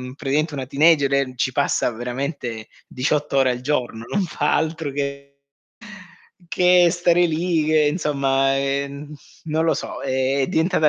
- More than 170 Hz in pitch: No, medium, 140 Hz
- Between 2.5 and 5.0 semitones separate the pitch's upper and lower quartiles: Yes, average, 2.9 semitones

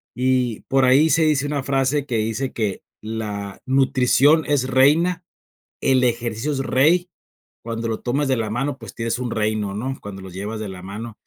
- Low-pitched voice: Yes, low, 125 Hz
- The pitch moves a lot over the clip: No, average, 3.9 semitones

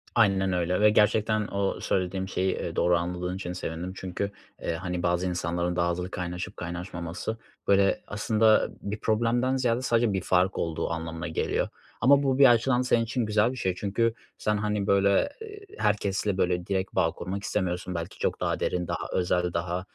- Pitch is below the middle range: Yes, very low, 95 Hz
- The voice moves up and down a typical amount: Yes, average, 3.4 semitones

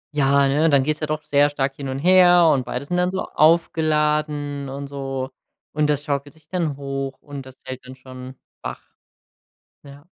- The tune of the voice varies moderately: No, narrow, 2.1 semitones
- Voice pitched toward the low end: No, medium, 145 Hz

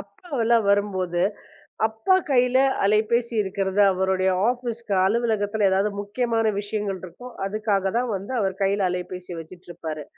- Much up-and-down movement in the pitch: No, average, 3.2 semitones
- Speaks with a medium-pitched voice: No, high, 205 Hz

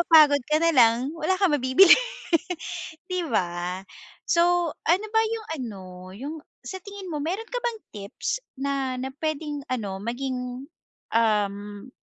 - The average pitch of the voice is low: No, very high, 285 Hz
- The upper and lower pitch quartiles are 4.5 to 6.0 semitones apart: No, wide, 6.9 semitones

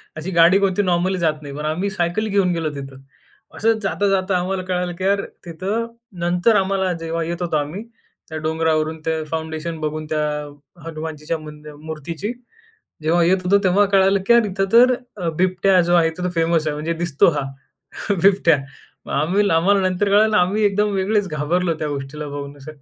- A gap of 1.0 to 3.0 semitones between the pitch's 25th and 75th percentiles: No, average, 3.6 semitones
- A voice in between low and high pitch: Yes, medium, 175 Hz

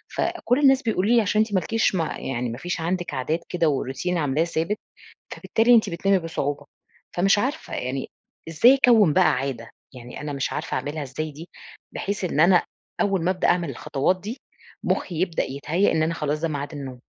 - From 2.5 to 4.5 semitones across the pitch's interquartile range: No, wide, 5.4 semitones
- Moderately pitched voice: Yes, medium, 165 Hz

